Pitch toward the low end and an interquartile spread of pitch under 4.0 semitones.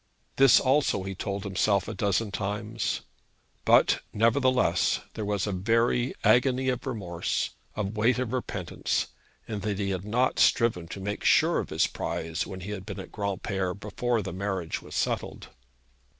Yes: low, 105 Hz; average, 3.4 semitones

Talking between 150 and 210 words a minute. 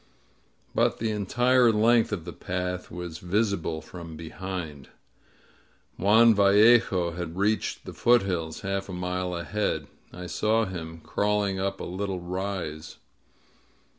No: slow, 135 wpm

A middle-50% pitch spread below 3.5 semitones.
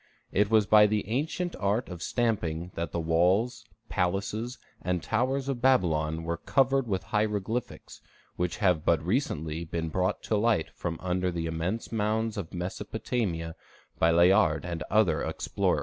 No: average, 4.9 semitones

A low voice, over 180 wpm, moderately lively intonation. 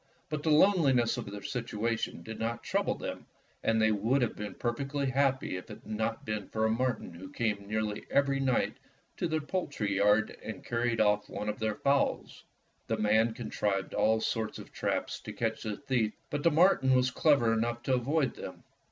Yes: low, 115 Hz; average, 195 wpm; average, 3.9 semitones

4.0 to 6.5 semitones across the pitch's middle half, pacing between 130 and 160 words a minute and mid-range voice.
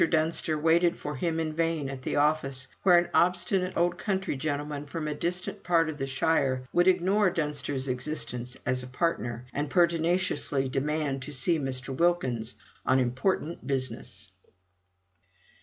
Yes: average, 4.4 semitones; average, 150 wpm; medium, 150 Hz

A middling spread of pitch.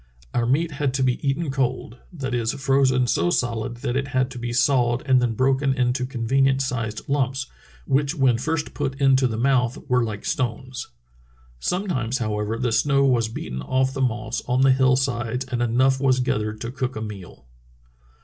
No: narrow, 2.2 semitones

